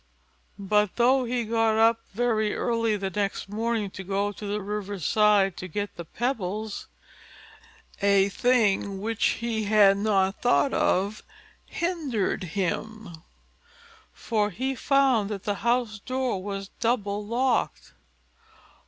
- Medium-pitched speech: No, high, 210 Hz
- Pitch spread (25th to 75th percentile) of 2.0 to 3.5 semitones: Yes, average, 2.8 semitones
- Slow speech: Yes, slow, 125 wpm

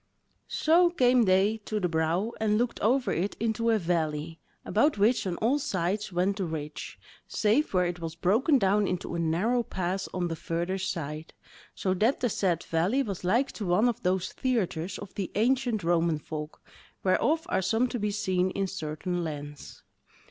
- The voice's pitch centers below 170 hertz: No, high, 190 Hz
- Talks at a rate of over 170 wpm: Yes, average, 180 wpm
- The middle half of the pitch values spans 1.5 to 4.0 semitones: No, average, 4.7 semitones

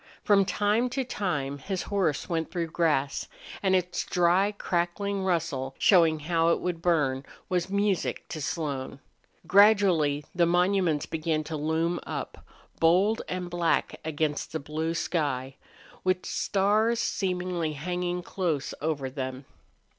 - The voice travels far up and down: No, average, 3.4 semitones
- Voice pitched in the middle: Yes, medium, 170 Hz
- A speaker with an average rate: No, slow, 130 wpm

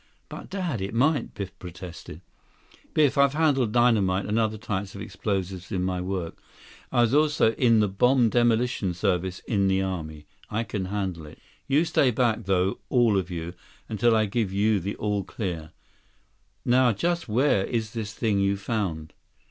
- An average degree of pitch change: Yes, average, 4.1 semitones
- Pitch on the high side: No, low, 105 Hz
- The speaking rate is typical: Yes, average, 170 wpm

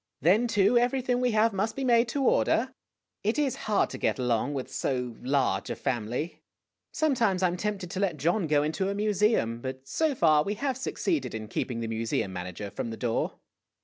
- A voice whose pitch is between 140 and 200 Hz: Yes, medium, 185 Hz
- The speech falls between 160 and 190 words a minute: No, fast, 205 wpm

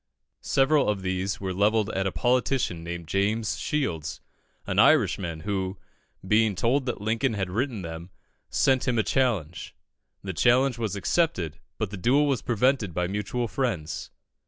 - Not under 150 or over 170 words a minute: Yes, average, 155 wpm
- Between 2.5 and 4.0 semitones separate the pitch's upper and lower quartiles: No, average, 5.1 semitones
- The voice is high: No, low, 105 Hz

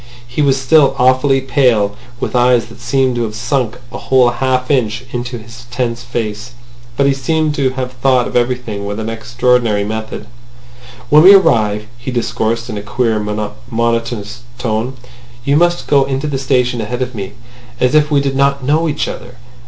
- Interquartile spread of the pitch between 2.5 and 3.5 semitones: Yes, average, 2.9 semitones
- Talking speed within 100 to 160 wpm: No, average, 175 wpm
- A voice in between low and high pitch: No, low, 125 Hz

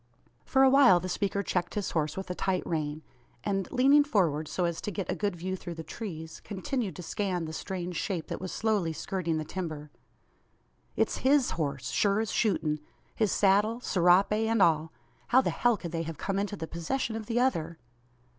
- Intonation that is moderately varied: Yes, average, 4.5 semitones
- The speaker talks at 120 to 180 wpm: No, average, 200 wpm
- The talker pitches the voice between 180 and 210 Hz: Yes, medium, 185 Hz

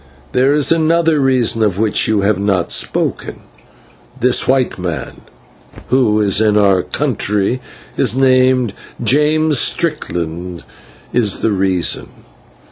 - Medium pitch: No, low, 115 Hz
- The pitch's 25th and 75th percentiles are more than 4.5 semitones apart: Yes, average, 5.2 semitones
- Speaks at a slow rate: Yes, slow, 120 wpm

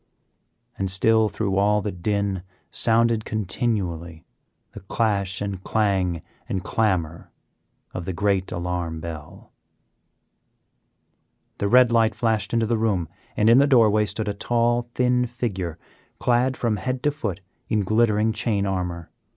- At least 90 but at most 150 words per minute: Yes, slow, 135 wpm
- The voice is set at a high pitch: No, low, 105 Hz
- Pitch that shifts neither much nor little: Yes, average, 3.6 semitones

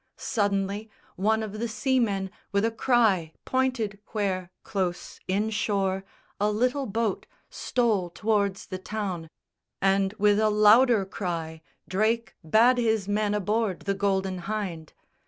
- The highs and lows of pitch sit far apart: No, narrow, 2.4 semitones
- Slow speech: Yes, slow, 125 wpm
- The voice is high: Yes, high, 205 Hz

